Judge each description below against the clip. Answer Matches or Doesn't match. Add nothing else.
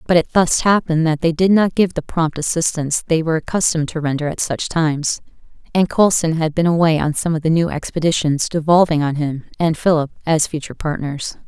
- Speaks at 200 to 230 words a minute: Matches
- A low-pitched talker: Doesn't match